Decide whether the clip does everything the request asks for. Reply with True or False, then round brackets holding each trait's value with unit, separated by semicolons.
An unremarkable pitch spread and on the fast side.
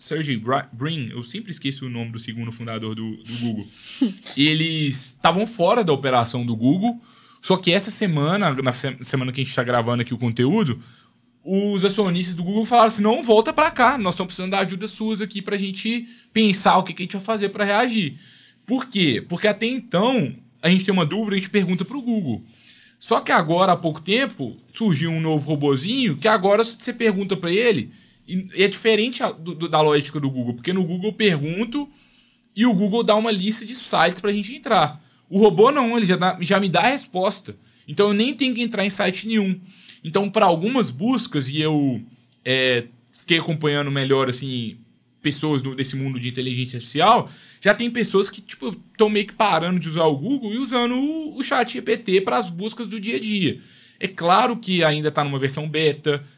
False (7.3 semitones; 205 wpm)